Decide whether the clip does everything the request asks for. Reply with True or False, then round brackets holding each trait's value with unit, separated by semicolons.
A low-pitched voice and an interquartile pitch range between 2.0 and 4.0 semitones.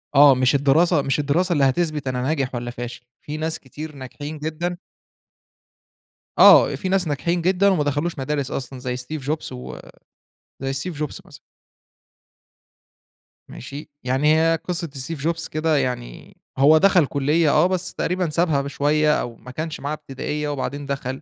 False (150 Hz; 3.2 semitones)